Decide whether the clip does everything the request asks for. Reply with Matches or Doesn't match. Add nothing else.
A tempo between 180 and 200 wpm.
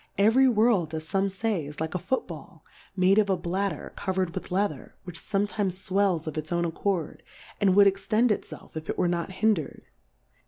Matches